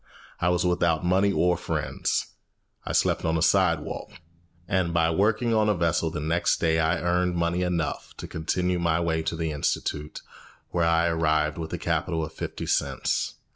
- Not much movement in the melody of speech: Yes, narrow, 1.7 semitones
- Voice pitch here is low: Yes, very low, 85 Hz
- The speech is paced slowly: No, average, 175 wpm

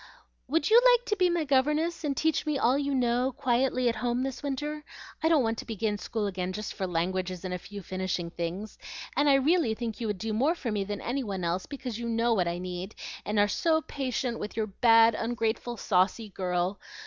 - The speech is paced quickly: Yes, fast, 220 wpm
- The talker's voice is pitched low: No, high, 230 Hz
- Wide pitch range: Yes, wide, 5.7 semitones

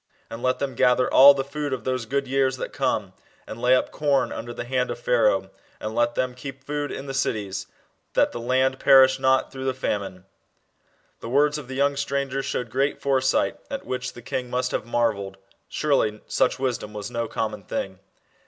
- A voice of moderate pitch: No, low, 130 Hz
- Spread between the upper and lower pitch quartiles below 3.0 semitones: Yes, narrow, 2.4 semitones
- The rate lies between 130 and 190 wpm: No, average, 200 wpm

